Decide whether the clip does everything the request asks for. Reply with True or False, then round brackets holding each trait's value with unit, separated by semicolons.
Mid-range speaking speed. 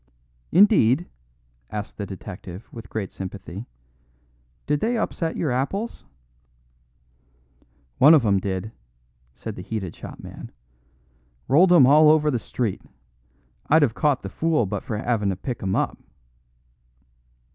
False (130 wpm)